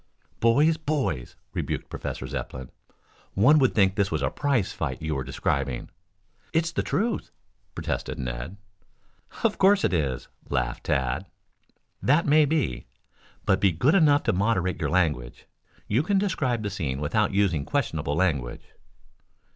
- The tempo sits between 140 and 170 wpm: Yes, average, 145 wpm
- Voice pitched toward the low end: Yes, low, 100 Hz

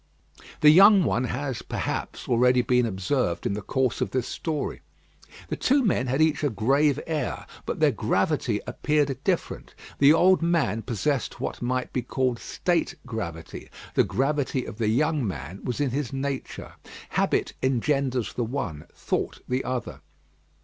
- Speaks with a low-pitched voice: Yes, low, 130 Hz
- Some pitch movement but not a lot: Yes, average, 3.7 semitones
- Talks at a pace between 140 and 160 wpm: Yes, average, 155 wpm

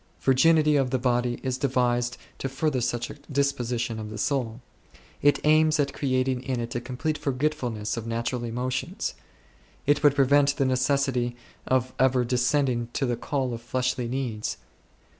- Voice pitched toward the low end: Yes, low, 130 Hz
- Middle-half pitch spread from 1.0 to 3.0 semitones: Yes, narrow, 2.5 semitones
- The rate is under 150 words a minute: No, average, 160 wpm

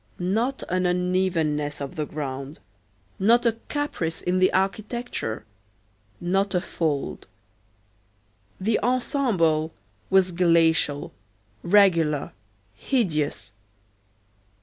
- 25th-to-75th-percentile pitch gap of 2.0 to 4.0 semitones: No, average, 4.6 semitones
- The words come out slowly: Yes, slow, 85 wpm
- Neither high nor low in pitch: Yes, medium, 180 Hz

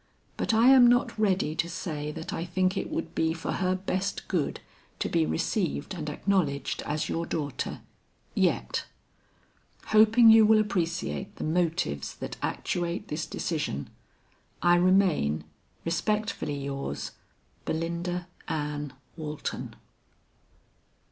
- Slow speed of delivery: Yes, slow, 120 wpm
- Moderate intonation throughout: Yes, average, 4.5 semitones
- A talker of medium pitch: Yes, medium, 170 Hz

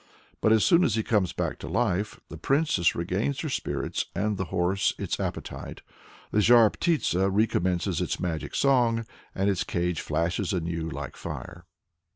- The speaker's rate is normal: Yes, average, 165 wpm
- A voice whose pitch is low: Yes, very low, 95 Hz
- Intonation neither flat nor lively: Yes, average, 4.7 semitones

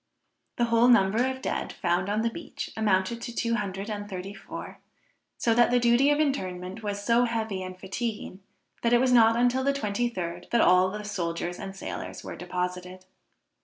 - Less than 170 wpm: No, average, 190 wpm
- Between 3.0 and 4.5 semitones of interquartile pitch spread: Yes, average, 4.2 semitones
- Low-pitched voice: No, high, 210 Hz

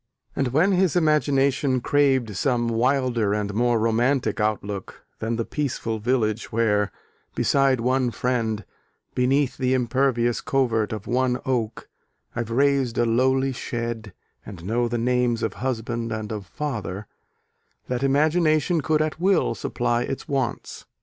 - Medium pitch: No, low, 125 Hz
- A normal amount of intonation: Yes, average, 3.2 semitones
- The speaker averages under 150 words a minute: Yes, slow, 135 wpm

